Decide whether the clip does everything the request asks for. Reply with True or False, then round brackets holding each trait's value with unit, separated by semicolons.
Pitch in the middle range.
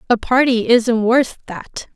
False (235 Hz)